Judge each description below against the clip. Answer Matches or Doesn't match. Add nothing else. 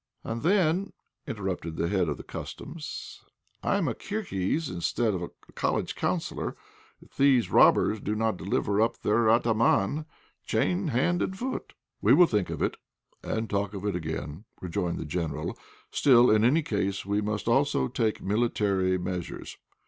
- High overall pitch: Doesn't match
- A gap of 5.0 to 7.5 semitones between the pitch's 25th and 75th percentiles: Matches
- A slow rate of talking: Doesn't match